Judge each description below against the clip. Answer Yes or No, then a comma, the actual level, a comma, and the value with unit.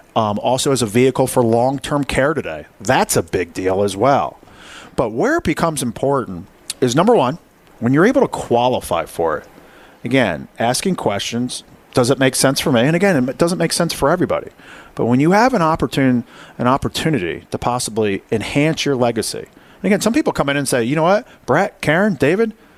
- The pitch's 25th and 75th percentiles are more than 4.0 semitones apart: Yes, average, 5.2 semitones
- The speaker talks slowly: No, average, 195 wpm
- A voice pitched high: No, medium, 140 Hz